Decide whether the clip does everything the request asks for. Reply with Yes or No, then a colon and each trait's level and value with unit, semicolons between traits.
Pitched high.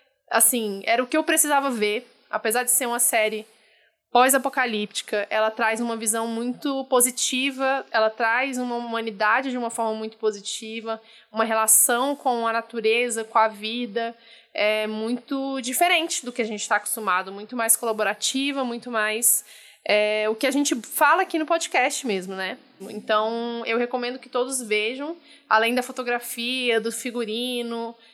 Yes: high, 230 Hz